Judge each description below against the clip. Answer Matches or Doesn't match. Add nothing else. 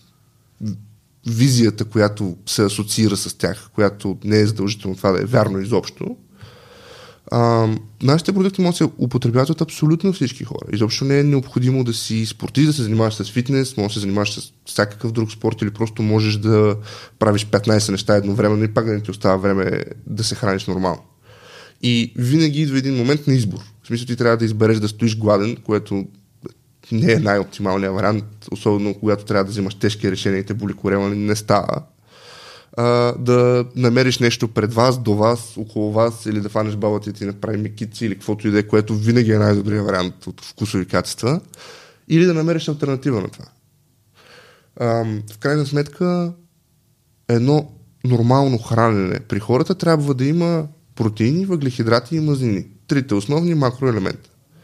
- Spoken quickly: Matches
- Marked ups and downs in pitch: Doesn't match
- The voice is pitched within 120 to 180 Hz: Doesn't match